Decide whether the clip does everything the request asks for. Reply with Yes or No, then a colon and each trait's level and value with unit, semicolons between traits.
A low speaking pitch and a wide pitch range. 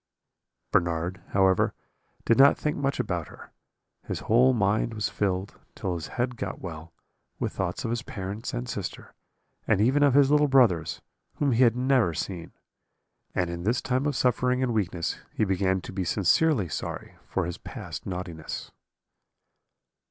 Yes: low, 105 Hz; wide, 5.8 semitones